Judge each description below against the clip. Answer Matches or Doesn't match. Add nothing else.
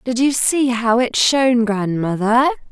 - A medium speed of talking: Matches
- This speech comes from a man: Doesn't match